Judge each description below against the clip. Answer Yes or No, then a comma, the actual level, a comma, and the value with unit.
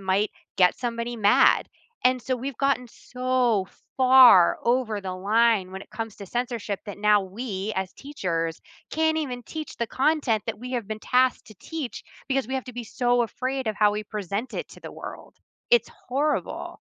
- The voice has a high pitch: Yes, high, 235 Hz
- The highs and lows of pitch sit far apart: No, average, 3.9 semitones